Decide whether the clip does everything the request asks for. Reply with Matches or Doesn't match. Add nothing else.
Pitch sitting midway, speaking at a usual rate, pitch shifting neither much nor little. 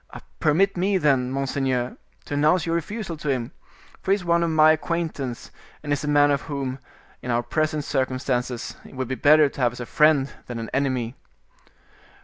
Matches